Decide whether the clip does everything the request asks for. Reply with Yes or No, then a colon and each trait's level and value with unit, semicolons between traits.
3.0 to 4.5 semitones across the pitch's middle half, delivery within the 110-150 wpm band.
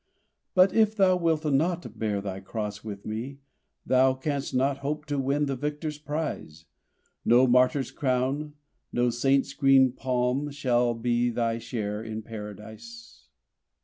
Yes: average, 4.2 semitones; average, 140 wpm